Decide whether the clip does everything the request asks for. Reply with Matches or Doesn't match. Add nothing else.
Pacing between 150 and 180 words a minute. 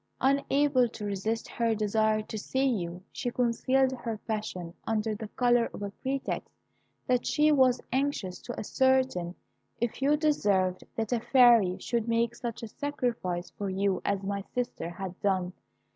Matches